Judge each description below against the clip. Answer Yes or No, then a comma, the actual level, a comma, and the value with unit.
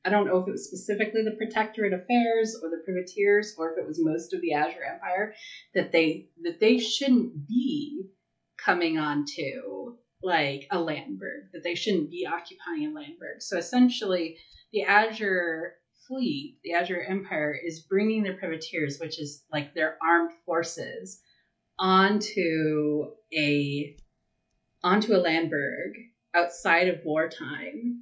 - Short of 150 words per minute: Yes, average, 140 wpm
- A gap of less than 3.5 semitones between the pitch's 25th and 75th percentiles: No, average, 5.1 semitones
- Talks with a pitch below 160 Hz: No, medium, 185 Hz